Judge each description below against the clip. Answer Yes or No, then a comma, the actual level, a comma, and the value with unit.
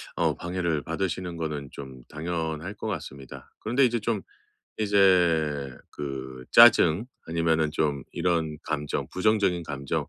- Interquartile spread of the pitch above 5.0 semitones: No, average, 4.1 semitones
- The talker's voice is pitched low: Yes, very low, 80 Hz